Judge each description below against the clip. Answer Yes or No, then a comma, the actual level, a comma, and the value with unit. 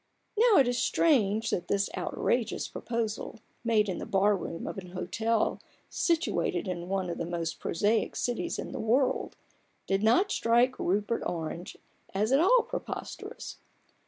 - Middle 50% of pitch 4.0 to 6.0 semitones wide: Yes, average, 4.4 semitones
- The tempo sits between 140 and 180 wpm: Yes, average, 155 wpm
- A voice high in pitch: Yes, high, 220 Hz